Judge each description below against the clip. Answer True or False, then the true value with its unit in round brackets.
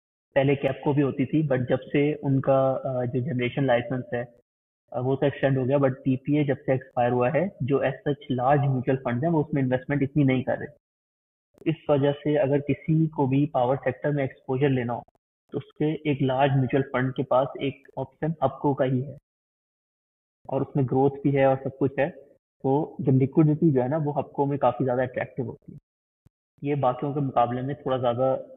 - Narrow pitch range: True (1.9 semitones)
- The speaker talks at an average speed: False (215 wpm)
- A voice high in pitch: False (135 Hz)